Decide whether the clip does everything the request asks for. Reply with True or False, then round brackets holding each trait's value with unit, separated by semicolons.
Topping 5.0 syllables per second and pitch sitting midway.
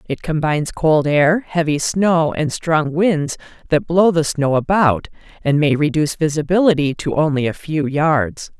False (4.4 syllables/s; 160 Hz)